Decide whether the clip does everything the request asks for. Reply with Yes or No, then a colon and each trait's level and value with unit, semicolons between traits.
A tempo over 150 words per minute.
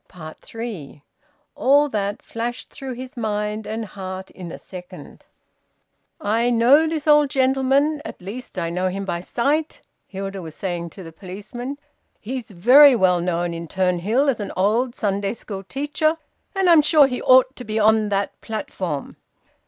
Yes: average, 160 wpm